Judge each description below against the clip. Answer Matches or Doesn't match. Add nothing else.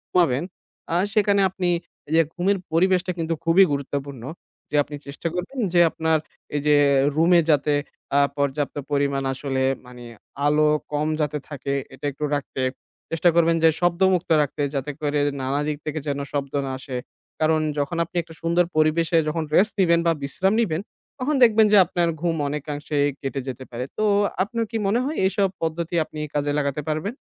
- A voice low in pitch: Doesn't match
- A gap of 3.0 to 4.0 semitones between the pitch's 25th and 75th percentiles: Matches